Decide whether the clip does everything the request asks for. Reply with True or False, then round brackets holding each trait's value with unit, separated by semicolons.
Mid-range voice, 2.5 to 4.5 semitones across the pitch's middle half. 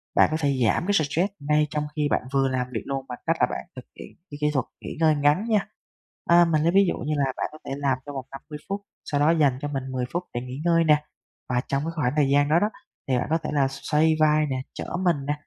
True (150 Hz; 2.9 semitones)